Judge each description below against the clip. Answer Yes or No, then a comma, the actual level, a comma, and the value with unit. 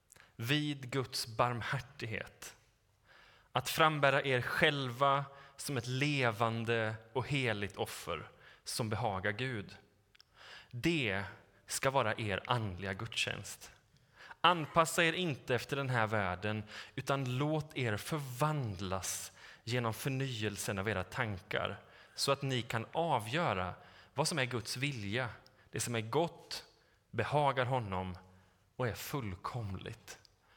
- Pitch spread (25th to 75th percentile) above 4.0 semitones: Yes, average, 4.8 semitones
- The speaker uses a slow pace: Yes, slow, 110 wpm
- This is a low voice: Yes, low, 120 Hz